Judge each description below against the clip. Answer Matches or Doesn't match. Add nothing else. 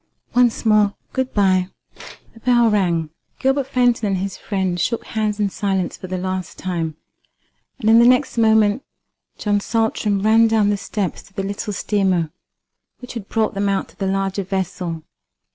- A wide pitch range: Doesn't match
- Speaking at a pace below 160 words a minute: Doesn't match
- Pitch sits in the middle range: Doesn't match